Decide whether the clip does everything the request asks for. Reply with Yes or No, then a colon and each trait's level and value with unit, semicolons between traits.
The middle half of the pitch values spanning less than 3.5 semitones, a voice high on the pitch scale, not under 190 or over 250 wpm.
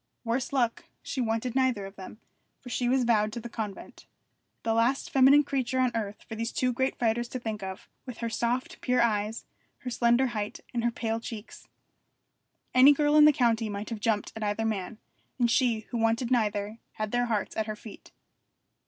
Yes: narrow, 2.5 semitones; high, 230 Hz; average, 195 wpm